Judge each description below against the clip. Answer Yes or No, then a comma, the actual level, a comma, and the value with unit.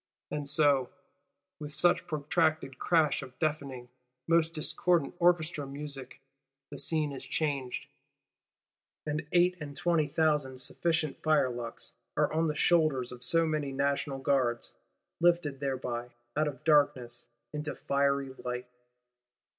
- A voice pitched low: No, medium, 145 Hz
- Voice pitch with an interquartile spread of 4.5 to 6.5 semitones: No, average, 2.9 semitones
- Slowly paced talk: Yes, slow, 125 wpm